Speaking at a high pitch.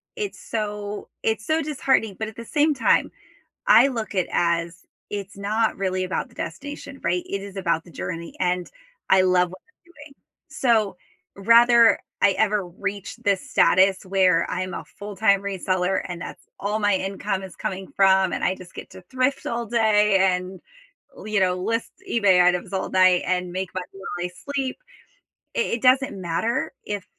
Yes: high, 195 Hz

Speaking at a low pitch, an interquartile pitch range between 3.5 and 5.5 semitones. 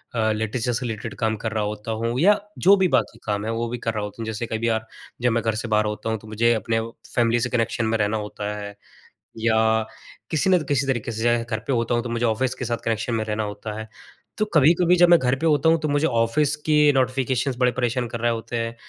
No: low, 115 Hz; average, 2.8 semitones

